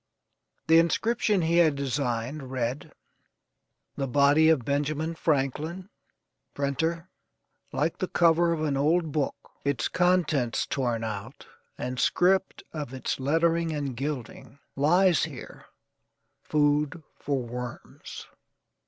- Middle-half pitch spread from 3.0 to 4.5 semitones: Yes, average, 3.7 semitones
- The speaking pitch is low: No, medium, 145 Hz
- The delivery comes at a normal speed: No, slow, 110 wpm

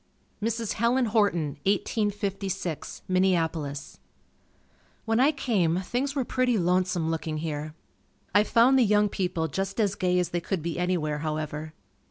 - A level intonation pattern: No, average, 5.0 semitones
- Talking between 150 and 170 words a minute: No, average, 140 wpm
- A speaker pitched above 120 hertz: Yes, medium, 185 Hz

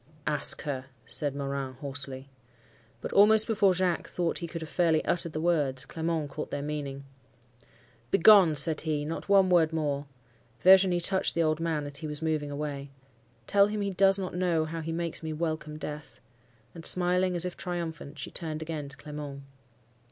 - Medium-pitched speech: Yes, medium, 160 Hz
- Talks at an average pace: Yes, average, 180 wpm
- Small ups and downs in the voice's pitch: No, average, 3.2 semitones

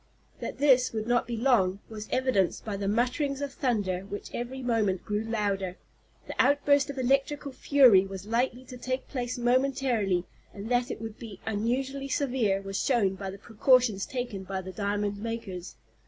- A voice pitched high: Yes, high, 230 Hz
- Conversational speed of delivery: Yes, average, 170 wpm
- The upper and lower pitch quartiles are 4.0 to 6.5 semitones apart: Yes, average, 4.5 semitones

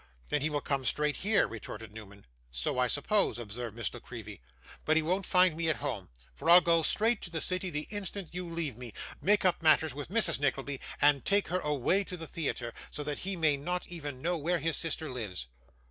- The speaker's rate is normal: No, fast, 220 wpm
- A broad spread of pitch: Yes, wide, 5.7 semitones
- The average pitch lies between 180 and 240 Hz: No, medium, 155 Hz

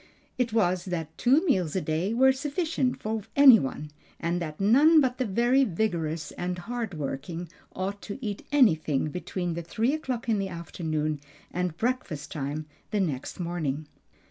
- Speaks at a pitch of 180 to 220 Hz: Yes, medium, 185 Hz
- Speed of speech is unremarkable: Yes, average, 160 wpm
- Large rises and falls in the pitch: Yes, wide, 7.0 semitones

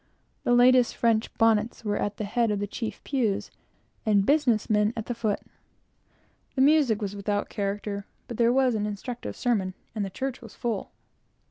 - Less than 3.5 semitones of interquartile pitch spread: Yes, average, 2.9 semitones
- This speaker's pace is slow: No, average, 175 wpm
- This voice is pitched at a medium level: No, high, 220 Hz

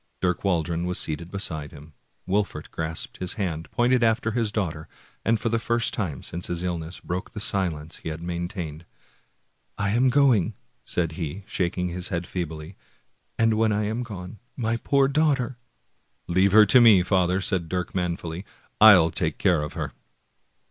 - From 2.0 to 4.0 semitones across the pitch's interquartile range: No, average, 4.5 semitones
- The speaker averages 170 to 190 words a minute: Yes, average, 180 wpm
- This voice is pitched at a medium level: No, very low, 90 Hz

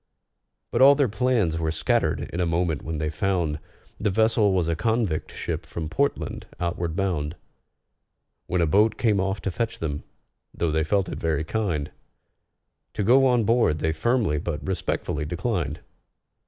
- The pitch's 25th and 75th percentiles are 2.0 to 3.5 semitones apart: No, wide, 5.6 semitones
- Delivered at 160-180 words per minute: Yes, average, 165 wpm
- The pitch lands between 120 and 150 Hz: No, very low, 90 Hz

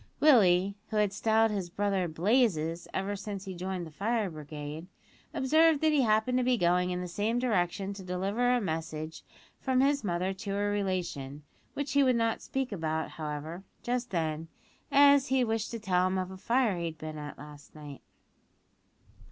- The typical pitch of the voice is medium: No, high, 195 Hz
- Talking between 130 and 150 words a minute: No, average, 185 wpm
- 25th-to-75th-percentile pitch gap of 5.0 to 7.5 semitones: Yes, wide, 5.6 semitones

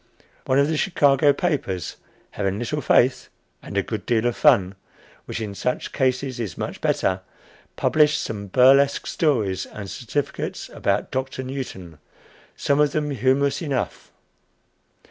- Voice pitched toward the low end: Yes, low, 130 Hz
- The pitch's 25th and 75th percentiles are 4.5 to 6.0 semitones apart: Yes, average, 4.9 semitones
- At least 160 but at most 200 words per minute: No, average, 140 wpm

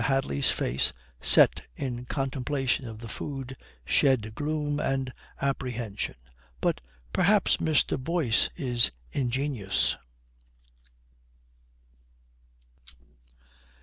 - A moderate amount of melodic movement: Yes, average, 3.3 semitones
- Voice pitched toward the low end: Yes, low, 130 Hz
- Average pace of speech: No, slow, 80 wpm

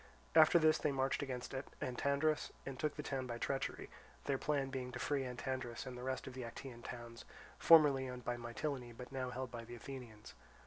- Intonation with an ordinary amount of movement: No, narrow, 2.2 semitones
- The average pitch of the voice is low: Yes, low, 130 Hz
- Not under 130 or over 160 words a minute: No, average, 195 wpm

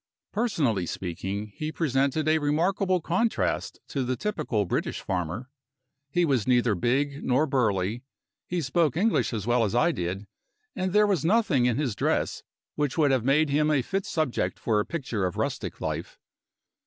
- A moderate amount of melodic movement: No, wide, 6.1 semitones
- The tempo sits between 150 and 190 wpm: Yes, average, 165 wpm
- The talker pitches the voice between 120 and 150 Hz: Yes, medium, 140 Hz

